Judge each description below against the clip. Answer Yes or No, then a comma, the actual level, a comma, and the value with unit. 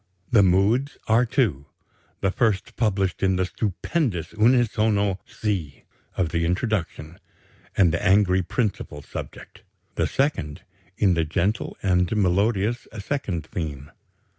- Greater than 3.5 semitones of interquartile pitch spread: Yes, average, 3.9 semitones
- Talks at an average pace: No, slow, 125 wpm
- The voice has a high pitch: No, very low, 95 Hz